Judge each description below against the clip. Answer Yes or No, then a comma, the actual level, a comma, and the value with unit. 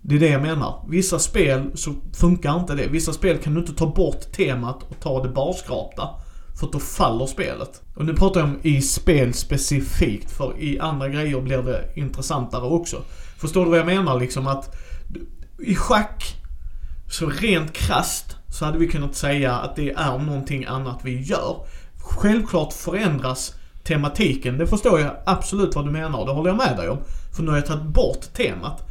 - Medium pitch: Yes, medium, 145 Hz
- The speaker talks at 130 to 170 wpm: No, average, 190 wpm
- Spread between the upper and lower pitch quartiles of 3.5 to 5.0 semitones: Yes, average, 4.0 semitones